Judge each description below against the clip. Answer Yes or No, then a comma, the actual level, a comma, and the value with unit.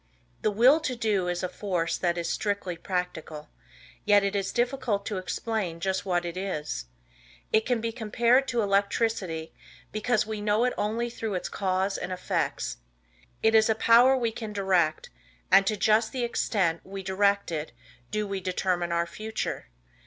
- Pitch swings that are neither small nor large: Yes, average, 3.6 semitones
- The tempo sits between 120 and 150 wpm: No, average, 170 wpm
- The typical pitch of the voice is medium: No, high, 200 Hz